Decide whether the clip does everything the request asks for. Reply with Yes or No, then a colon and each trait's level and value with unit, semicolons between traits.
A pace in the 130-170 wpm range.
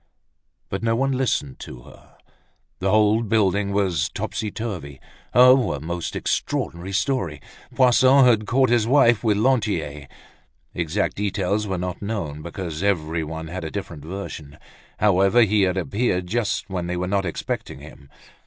Yes: average, 150 wpm